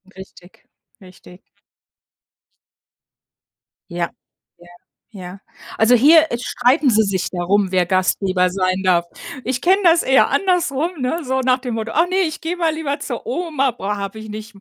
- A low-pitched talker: No, high, 235 Hz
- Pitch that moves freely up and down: Yes, wide, 8.5 semitones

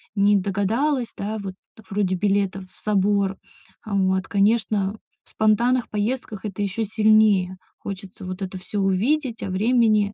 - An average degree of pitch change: No, narrow, 2.1 semitones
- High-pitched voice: Yes, high, 205 Hz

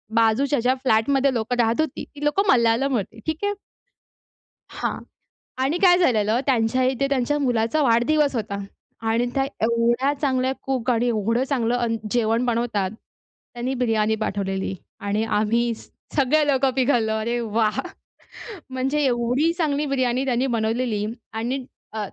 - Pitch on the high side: Yes, high, 245 Hz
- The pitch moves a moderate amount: Yes, average, 3.2 semitones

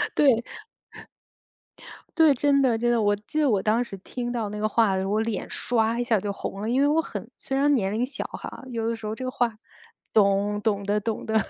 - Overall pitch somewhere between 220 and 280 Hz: Yes, high, 225 Hz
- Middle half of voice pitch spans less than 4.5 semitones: Yes, average, 3.0 semitones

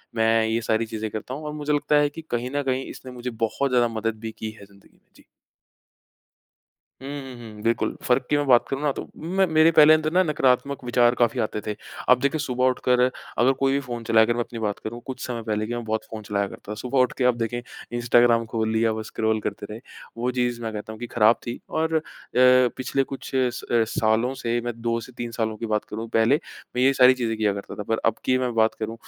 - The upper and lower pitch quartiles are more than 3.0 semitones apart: No, average, 2.7 semitones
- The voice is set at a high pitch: No, low, 120 Hz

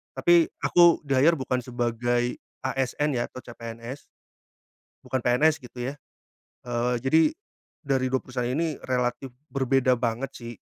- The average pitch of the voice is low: Yes, low, 130 Hz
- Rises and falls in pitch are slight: Yes, narrow, 2.2 semitones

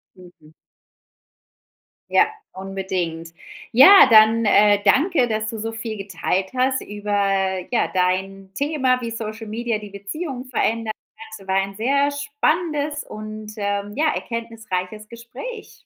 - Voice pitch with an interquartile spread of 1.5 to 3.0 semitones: No, average, 4.5 semitones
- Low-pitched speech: No, high, 220 Hz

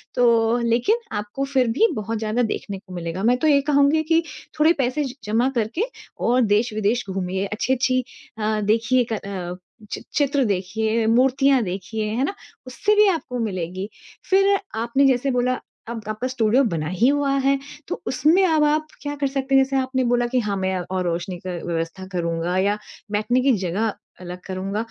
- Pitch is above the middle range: Yes, high, 235 Hz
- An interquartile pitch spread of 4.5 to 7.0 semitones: Yes, average, 5.1 semitones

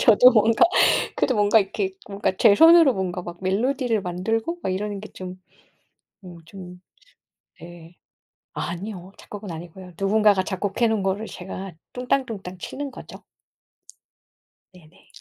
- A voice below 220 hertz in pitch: Yes, high, 195 Hz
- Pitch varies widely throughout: No, average, 3.5 semitones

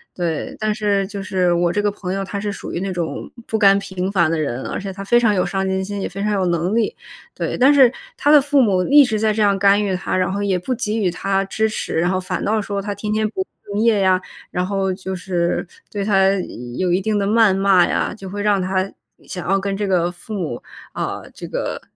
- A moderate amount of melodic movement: No, narrow, 2.2 semitones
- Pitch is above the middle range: Yes, high, 195 Hz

